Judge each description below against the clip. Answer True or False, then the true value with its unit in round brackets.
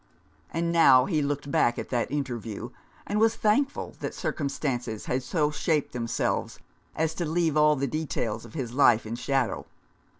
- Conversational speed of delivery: True (165 wpm)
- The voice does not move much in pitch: False (4.7 semitones)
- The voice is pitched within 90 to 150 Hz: True (140 Hz)